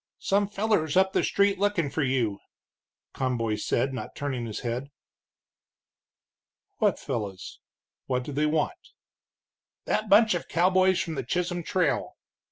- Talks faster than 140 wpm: No, slow, 135 wpm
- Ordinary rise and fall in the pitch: No, wide, 7.0 semitones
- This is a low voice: No, medium, 155 Hz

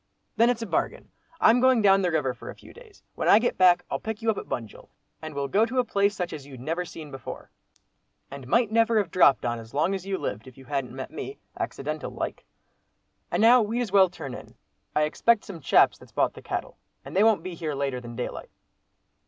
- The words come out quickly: Yes, fast, 235 wpm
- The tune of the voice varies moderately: No, wide, 8.0 semitones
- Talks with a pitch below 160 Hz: No, medium, 180 Hz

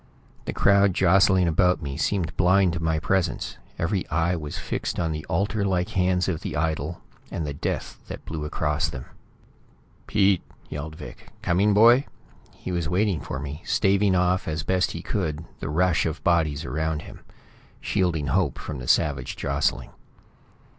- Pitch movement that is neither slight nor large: Yes, average, 3.4 semitones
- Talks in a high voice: No, very low, 85 Hz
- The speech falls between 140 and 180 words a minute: Yes, average, 165 wpm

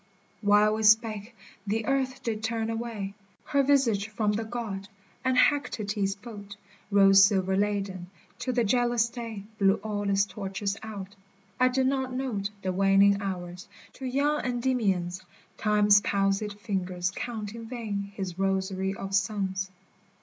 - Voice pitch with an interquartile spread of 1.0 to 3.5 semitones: Yes, average, 3.0 semitones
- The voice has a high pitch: Yes, high, 205 Hz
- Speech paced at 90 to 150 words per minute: Yes, average, 140 wpm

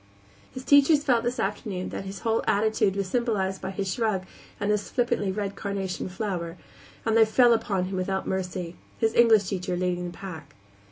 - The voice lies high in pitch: Yes, high, 195 Hz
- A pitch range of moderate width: Yes, average, 3.2 semitones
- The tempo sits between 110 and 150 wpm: No, average, 180 wpm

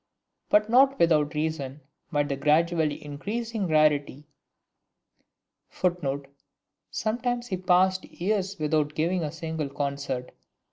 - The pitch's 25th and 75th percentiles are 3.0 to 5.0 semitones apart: Yes, average, 4.4 semitones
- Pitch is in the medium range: Yes, medium, 160 Hz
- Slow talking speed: Yes, slow, 105 wpm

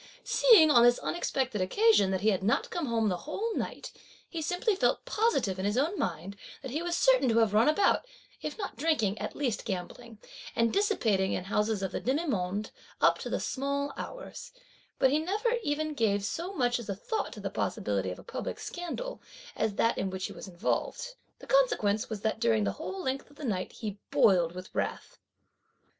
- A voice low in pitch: No, high, 240 Hz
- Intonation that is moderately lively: No, wide, 8.4 semitones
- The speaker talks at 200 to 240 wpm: Yes, fast, 205 wpm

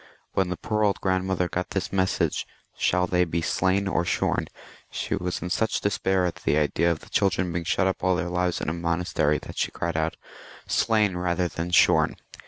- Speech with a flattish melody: Yes, narrow, 1.7 semitones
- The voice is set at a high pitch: No, very low, 90 Hz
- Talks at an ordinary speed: No, fast, 215 wpm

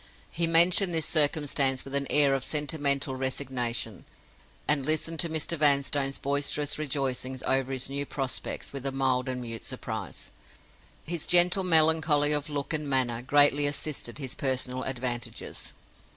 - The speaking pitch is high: No, medium, 140 Hz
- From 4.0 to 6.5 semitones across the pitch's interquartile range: No, narrow, 2.5 semitones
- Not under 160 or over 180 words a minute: No, average, 145 wpm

